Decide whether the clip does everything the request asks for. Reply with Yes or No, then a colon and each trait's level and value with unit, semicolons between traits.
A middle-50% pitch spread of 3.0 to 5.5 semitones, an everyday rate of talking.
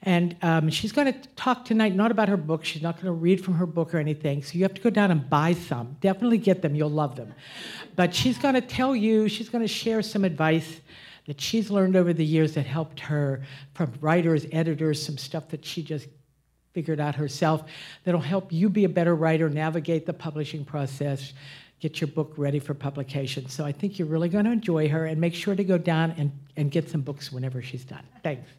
No: average, 4.0 semitones; fast, 220 wpm